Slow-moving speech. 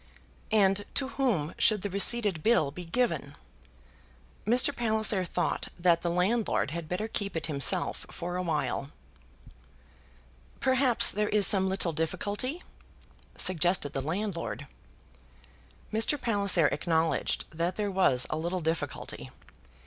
Yes: slow, 125 wpm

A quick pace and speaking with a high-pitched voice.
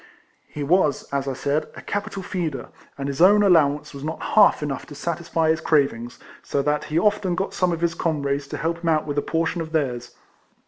No: fast, 230 wpm; medium, 155 Hz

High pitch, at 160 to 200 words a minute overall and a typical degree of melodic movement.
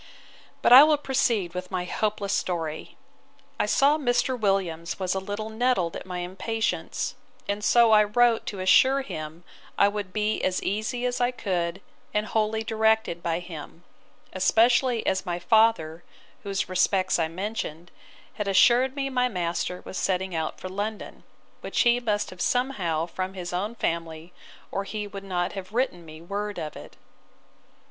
Yes: high, 200 Hz; average, 165 wpm; average, 4.1 semitones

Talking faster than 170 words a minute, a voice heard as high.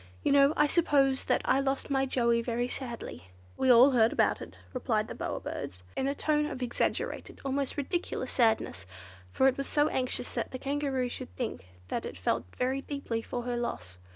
Yes: average, 195 wpm; very high, 260 Hz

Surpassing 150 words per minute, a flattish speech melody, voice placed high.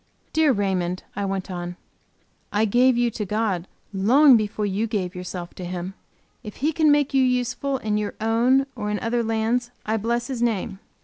No: average, 185 wpm; average, 4.1 semitones; high, 220 Hz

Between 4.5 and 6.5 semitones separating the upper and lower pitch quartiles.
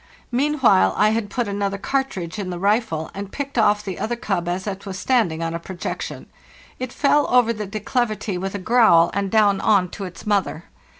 No: average, 3.8 semitones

